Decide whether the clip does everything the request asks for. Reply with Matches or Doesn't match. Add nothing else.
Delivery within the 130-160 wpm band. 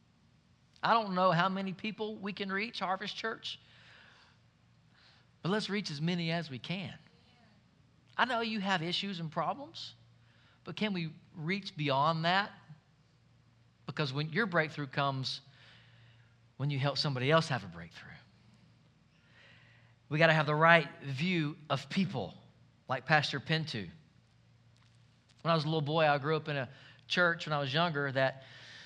Matches